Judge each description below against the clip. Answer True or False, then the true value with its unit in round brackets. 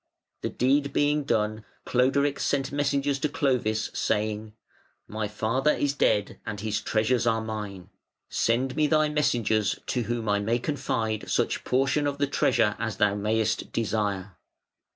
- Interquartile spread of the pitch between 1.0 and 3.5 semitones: False (4.5 semitones)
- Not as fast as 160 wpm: True (150 wpm)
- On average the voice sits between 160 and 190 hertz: False (115 Hz)